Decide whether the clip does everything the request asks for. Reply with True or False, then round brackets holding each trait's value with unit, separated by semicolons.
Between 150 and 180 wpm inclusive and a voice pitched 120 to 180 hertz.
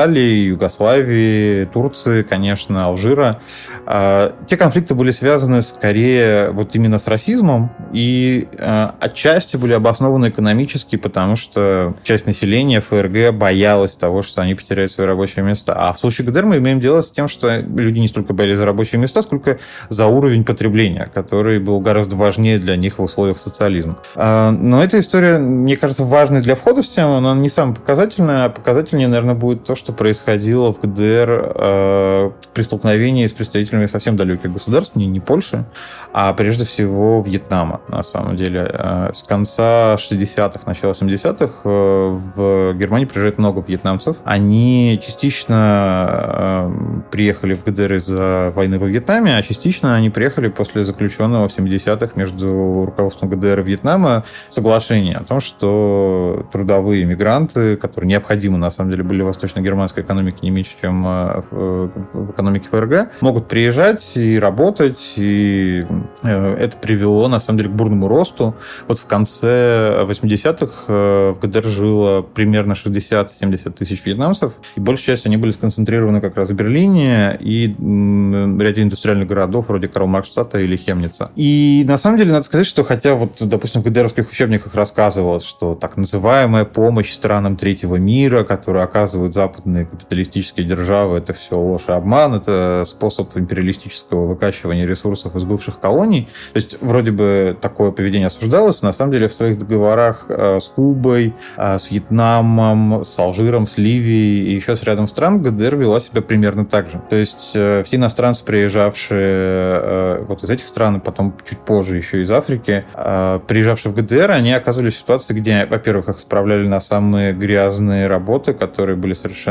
False (155 wpm; 105 Hz)